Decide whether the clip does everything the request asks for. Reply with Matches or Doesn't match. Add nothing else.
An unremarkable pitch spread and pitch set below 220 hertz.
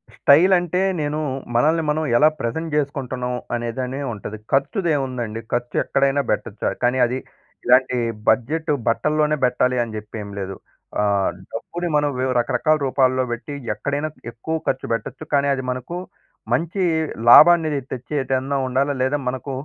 Matches